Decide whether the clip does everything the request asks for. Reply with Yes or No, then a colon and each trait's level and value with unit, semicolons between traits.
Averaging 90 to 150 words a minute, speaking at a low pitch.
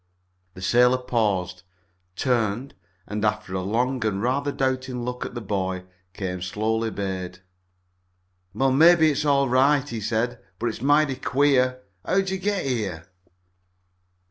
Yes: average, 140 wpm; low, 120 Hz